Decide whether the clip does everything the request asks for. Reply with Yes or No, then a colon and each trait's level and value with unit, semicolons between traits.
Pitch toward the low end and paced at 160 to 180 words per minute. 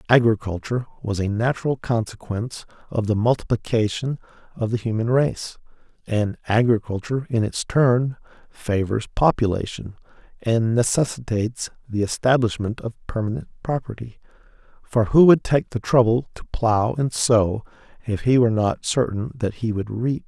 No: low, 115 Hz; slow, 135 wpm